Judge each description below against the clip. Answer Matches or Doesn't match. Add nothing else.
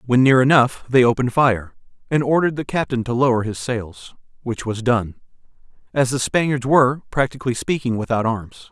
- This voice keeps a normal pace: Matches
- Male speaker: Matches